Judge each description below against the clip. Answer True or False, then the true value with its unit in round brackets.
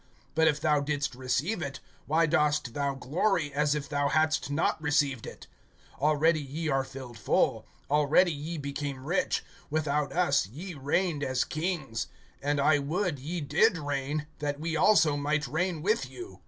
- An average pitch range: False (2.3 semitones)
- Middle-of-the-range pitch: True (150 Hz)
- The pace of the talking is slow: False (165 wpm)